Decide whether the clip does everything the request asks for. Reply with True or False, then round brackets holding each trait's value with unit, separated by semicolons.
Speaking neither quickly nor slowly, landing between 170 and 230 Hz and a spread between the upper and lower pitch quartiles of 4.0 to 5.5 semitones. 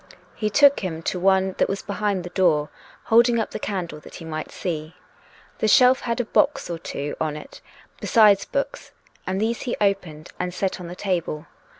True (195 wpm; 190 Hz; 4.4 semitones)